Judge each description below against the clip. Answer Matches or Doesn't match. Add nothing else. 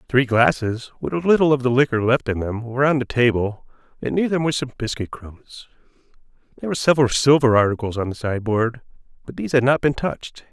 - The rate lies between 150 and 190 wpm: Doesn't match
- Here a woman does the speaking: Doesn't match